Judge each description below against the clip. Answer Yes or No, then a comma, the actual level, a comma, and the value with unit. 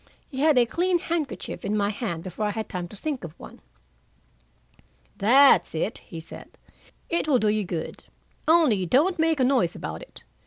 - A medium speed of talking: Yes, average, 185 wpm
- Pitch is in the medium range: No, high, 230 Hz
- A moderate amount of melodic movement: No, wide, 8.1 semitones